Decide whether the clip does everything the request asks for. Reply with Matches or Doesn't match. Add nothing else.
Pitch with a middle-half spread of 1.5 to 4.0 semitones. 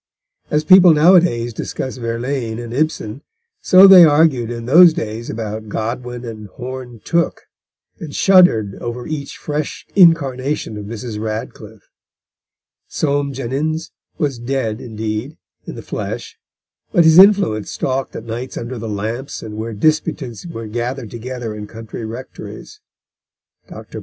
Doesn't match